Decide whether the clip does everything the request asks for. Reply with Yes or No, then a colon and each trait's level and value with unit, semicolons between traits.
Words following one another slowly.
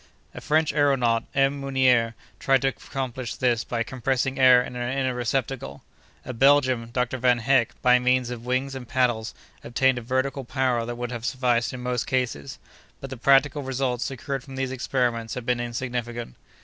No: average, 175 wpm